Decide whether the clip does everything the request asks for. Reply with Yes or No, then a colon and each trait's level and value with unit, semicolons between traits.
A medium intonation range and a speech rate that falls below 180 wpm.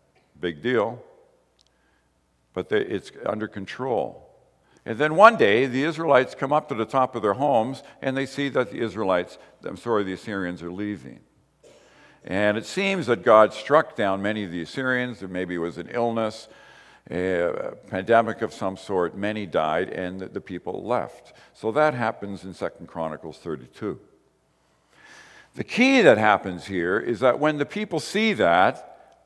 No: wide, 6.5 semitones; average, 160 wpm